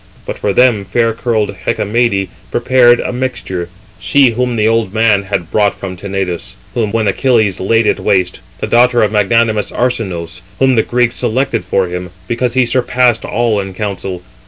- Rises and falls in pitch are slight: No, average, 3.7 semitones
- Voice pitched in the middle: No, low, 110 Hz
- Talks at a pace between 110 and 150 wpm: No, average, 165 wpm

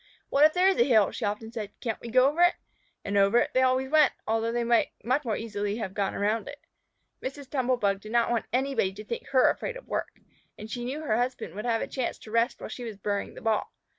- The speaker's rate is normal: No, fast, 255 wpm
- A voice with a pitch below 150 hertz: No, high, 235 Hz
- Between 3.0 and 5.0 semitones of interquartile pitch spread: Yes, average, 3.5 semitones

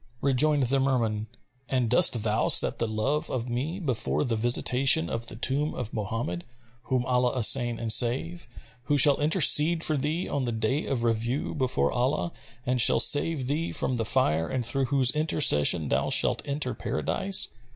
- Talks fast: No, average, 170 wpm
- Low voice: Yes, low, 125 Hz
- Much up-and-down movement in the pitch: No, average, 3.8 semitones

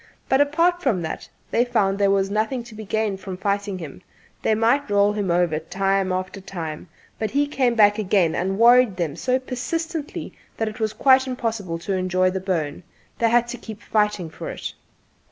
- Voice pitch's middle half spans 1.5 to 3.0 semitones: No, average, 4.4 semitones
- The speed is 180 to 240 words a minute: Yes, average, 195 wpm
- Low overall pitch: No, high, 205 Hz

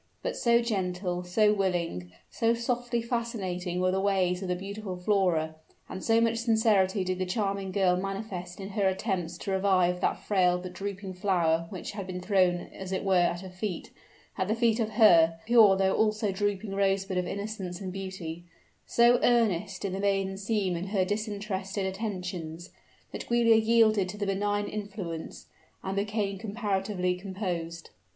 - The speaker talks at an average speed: Yes, average, 170 wpm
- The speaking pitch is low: No, high, 195 Hz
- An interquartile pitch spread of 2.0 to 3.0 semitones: Yes, narrow, 2.6 semitones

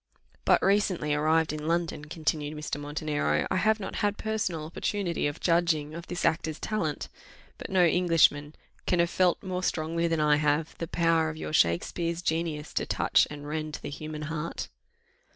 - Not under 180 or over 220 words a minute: No, average, 170 wpm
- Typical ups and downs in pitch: No, narrow, 2.3 semitones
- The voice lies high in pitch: No, medium, 160 Hz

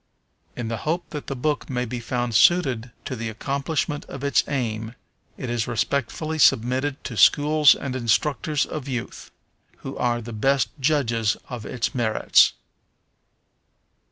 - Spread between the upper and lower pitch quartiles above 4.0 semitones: No, average, 3.7 semitones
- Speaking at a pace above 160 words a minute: No, average, 145 wpm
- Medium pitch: No, low, 125 Hz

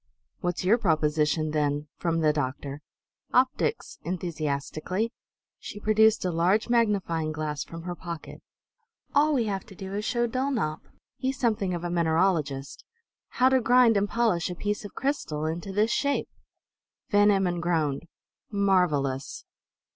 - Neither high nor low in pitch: Yes, medium, 180 Hz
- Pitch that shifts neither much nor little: No, wide, 5.9 semitones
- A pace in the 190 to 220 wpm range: No, average, 145 wpm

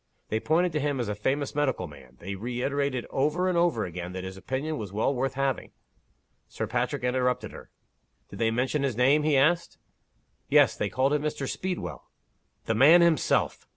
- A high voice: No, low, 135 Hz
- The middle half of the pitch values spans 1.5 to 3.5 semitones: No, average, 4.8 semitones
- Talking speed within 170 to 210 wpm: Yes, average, 190 wpm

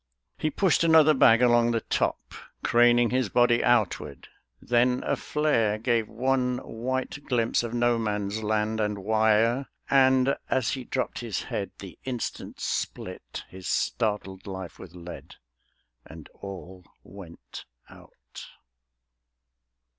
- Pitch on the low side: Yes, low, 115 Hz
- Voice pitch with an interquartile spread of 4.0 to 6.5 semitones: No, average, 3.3 semitones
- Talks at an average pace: No, slow, 125 wpm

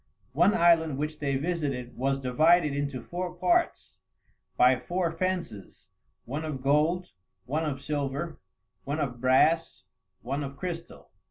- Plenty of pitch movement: No, average, 3.9 semitones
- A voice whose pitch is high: No, medium, 150 Hz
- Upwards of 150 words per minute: No, slow, 135 wpm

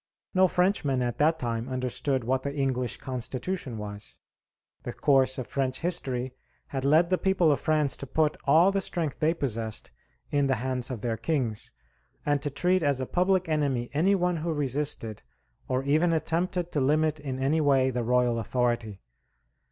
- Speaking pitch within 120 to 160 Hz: Yes, medium, 140 Hz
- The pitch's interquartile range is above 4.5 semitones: No, average, 4.2 semitones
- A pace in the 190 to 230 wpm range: No, average, 175 wpm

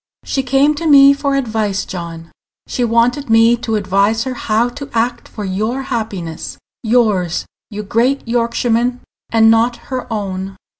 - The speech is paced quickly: No, average, 150 wpm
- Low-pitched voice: No, high, 230 Hz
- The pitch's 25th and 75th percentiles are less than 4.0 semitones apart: Yes, average, 3.3 semitones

